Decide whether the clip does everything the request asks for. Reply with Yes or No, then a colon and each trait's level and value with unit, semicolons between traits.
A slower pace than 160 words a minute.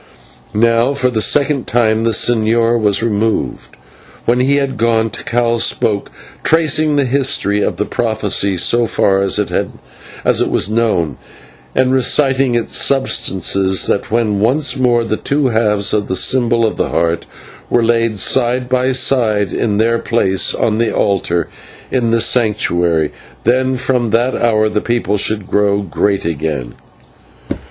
Yes: average, 150 wpm